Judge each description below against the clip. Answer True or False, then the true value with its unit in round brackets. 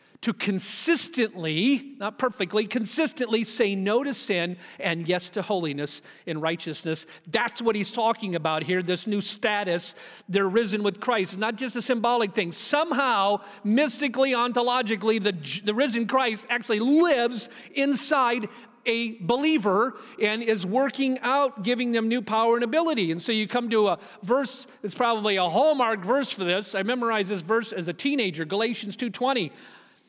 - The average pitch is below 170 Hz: False (225 Hz)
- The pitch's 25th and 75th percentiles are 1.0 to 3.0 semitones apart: False (3.9 semitones)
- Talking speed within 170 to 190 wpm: False (155 wpm)